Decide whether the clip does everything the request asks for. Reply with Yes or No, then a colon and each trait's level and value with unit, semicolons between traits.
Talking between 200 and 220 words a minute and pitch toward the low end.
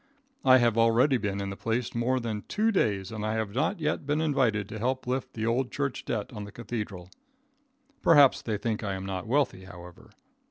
Yes: fast, 205 wpm; low, 115 Hz